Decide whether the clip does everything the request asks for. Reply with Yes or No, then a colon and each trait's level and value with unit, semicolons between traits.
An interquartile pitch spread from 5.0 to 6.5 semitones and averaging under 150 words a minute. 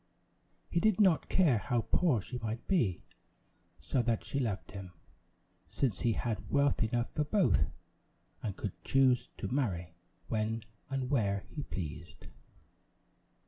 Yes: wide, 5.4 semitones; average, 140 wpm